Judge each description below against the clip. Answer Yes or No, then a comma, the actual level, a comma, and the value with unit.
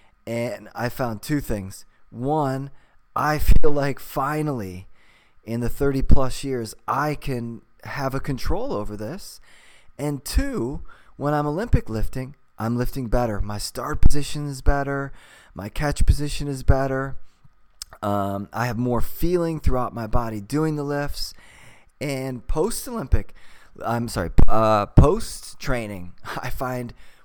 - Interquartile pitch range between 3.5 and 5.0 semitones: Yes, average, 4.4 semitones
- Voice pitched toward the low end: Yes, low, 125 Hz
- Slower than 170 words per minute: Yes, slow, 135 wpm